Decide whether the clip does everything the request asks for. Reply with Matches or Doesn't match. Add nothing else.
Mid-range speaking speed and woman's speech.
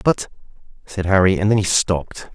Doesn't match